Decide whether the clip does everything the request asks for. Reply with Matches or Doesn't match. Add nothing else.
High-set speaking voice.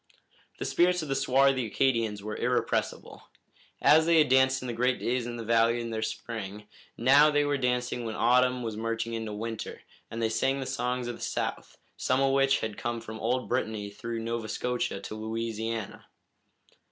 Doesn't match